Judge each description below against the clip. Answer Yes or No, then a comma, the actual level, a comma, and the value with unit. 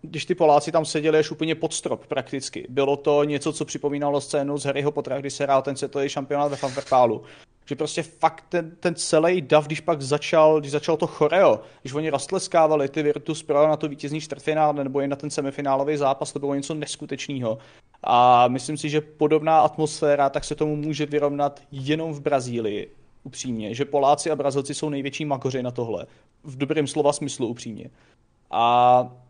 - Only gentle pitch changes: Yes, narrow, 1.9 semitones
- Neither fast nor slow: No, fast, 185 wpm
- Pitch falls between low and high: Yes, medium, 145 Hz